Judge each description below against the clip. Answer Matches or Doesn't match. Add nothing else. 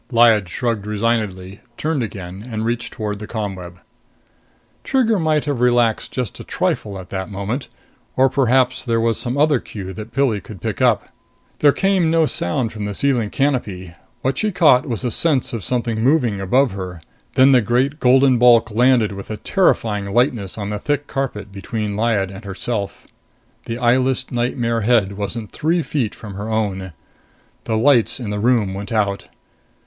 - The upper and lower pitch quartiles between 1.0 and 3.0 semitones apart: Doesn't match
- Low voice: Matches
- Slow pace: Doesn't match